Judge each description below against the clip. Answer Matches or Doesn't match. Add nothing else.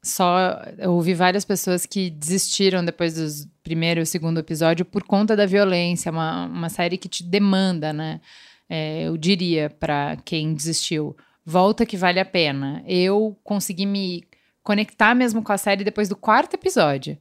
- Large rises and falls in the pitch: Doesn't match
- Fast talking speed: Doesn't match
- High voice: Doesn't match